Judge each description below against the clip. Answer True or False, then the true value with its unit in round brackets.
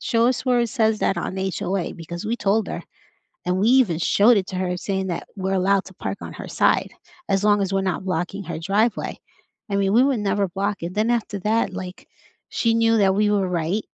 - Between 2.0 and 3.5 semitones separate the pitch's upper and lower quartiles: True (2.7 semitones)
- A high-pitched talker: True (195 Hz)